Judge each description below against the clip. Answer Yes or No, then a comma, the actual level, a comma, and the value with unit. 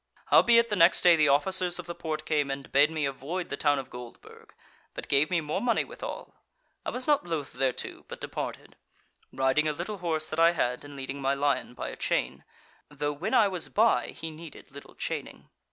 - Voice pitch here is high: No, medium, 155 Hz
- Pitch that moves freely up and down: No, average, 3.9 semitones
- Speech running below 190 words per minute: No, fast, 205 wpm